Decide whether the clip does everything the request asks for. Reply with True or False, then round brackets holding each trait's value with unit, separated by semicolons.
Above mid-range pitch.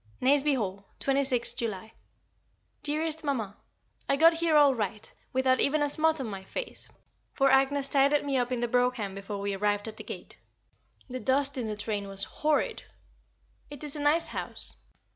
True (260 Hz)